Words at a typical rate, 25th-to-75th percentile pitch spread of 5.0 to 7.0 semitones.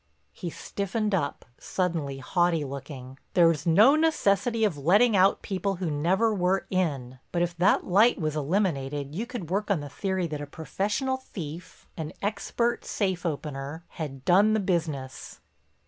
Yes: average, 145 wpm; average, 5.3 semitones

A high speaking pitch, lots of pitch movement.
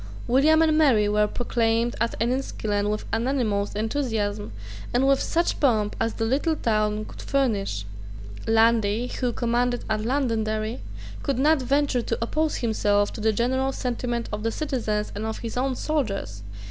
No: high, 230 Hz; average, 3.6 semitones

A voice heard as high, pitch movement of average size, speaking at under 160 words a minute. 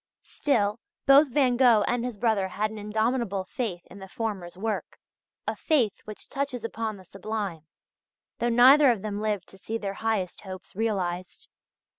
No: high, 215 Hz; average, 3.5 semitones; average, 165 wpm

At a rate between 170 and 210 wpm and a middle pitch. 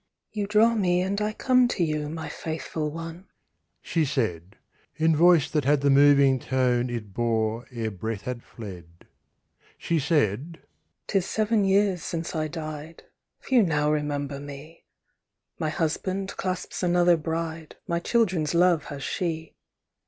No: average, 145 wpm; medium, 160 Hz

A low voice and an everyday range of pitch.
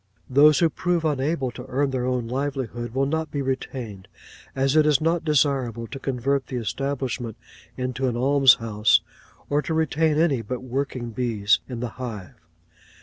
Yes: low, 130 Hz; average, 3.0 semitones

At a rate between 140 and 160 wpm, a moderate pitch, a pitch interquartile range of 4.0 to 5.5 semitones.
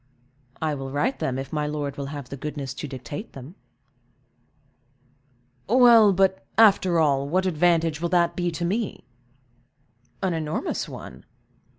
Yes: average, 145 wpm; medium, 160 Hz; average, 4.6 semitones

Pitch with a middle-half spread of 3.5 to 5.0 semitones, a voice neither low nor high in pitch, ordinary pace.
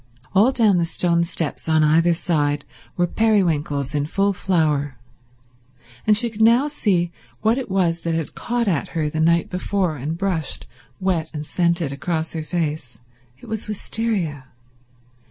Yes: average, 4.3 semitones; medium, 170 Hz; average, 155 wpm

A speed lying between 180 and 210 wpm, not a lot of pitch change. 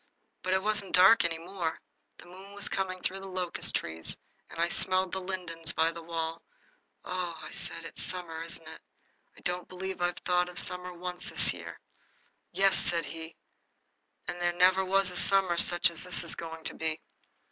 Yes: average, 190 wpm; narrow, 2.0 semitones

